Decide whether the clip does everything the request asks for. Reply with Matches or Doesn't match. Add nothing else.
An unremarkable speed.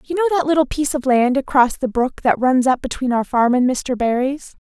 Doesn't match